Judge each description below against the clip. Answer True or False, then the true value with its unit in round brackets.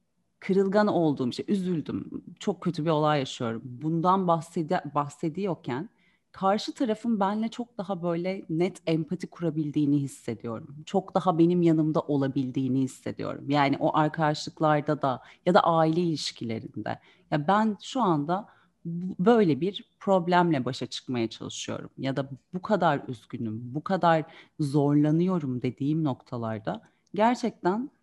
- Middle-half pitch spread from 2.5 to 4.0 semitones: False (4.8 semitones)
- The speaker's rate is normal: False (125 wpm)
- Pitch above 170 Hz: False (160 Hz)